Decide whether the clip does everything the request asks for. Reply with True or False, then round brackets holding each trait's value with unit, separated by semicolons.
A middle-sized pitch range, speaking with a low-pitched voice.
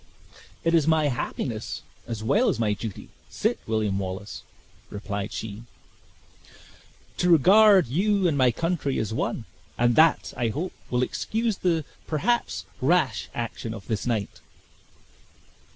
False (7.5 semitones; 125 Hz)